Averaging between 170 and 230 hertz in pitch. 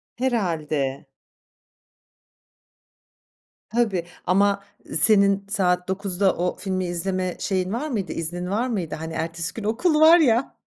Yes: high, 190 Hz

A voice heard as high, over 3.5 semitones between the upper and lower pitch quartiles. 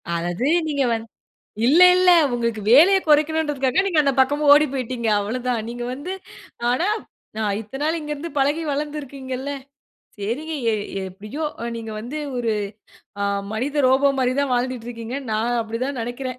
Yes: very high, 260 Hz; average, 4.0 semitones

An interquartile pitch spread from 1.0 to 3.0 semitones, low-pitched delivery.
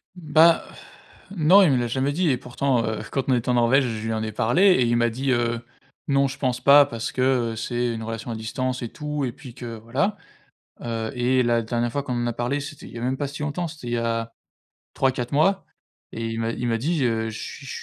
No: average, 3.4 semitones; low, 125 Hz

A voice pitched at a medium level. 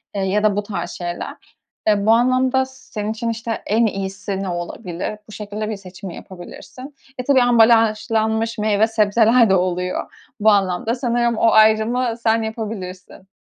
No: high, 215 Hz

